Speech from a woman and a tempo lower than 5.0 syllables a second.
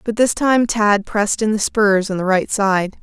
Yes: female; 4.5 syllables/s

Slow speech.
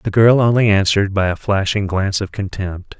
No: average, 200 wpm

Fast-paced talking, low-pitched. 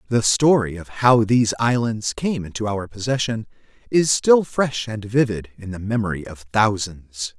No: average, 165 wpm; low, 110 Hz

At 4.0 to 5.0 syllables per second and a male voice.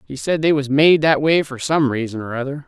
No: 5.6 syllables/s; male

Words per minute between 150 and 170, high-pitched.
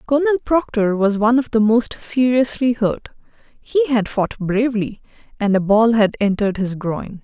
Yes: average, 165 wpm; high, 225 Hz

